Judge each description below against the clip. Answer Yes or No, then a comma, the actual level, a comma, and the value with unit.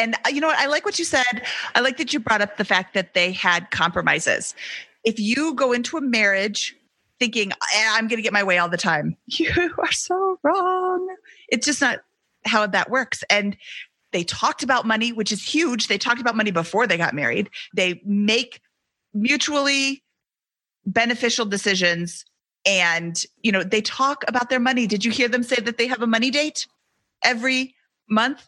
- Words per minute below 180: No, average, 185 wpm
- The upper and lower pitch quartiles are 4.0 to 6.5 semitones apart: Yes, average, 4.5 semitones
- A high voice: Yes, high, 235 Hz